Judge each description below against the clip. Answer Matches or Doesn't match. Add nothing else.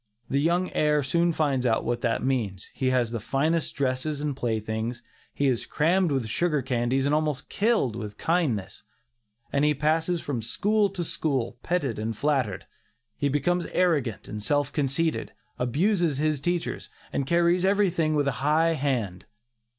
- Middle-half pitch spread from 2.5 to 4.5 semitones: Doesn't match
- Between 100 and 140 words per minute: Doesn't match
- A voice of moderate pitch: Matches